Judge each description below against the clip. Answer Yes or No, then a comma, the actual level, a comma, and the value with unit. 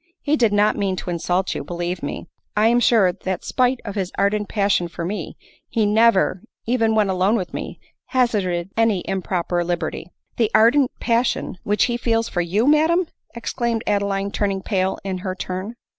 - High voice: Yes, high, 205 Hz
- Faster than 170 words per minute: Yes, average, 185 wpm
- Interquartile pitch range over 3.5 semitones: Yes, average, 3.9 semitones